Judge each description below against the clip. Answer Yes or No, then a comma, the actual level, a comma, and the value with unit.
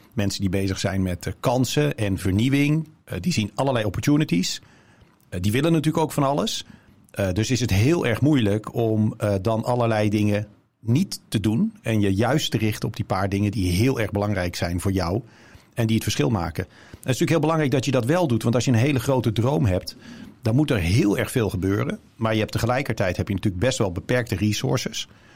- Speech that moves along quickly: Yes, fast, 210 wpm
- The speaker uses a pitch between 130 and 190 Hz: No, low, 110 Hz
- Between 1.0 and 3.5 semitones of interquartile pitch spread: No, average, 4.3 semitones